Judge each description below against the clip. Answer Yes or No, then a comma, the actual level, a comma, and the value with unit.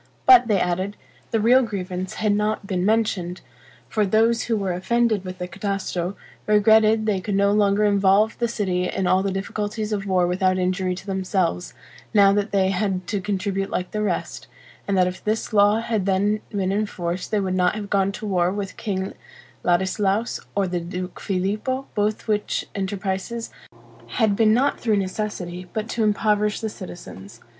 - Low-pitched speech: No, high, 200 Hz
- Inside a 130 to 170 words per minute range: No, average, 180 wpm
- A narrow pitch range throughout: Yes, narrow, 2.3 semitones